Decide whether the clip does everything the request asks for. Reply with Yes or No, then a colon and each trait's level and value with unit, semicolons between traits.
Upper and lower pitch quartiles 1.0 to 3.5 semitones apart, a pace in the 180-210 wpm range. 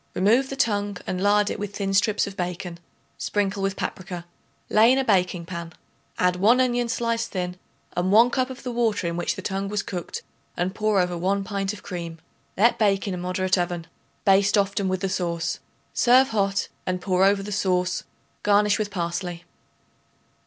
Yes: narrow, 2.5 semitones; average, 190 wpm